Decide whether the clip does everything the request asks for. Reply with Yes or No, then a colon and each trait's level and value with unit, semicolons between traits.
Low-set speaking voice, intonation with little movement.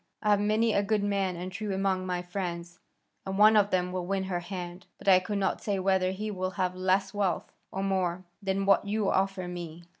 No: high, 190 Hz; narrow, 1.6 semitones